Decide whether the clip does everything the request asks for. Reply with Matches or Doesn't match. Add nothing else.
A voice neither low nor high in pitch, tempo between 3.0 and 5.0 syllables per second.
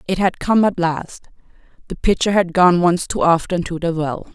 Matches